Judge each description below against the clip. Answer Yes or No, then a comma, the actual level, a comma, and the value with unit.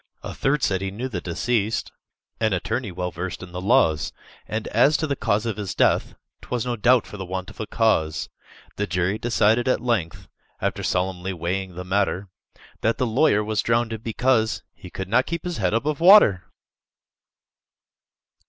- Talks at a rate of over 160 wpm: Yes, average, 180 wpm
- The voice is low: Yes, low, 105 Hz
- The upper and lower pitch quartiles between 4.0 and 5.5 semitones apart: Yes, average, 4.5 semitones